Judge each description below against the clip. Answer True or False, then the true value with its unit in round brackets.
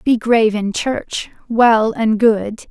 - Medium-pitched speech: False (225 Hz)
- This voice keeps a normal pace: True (155 wpm)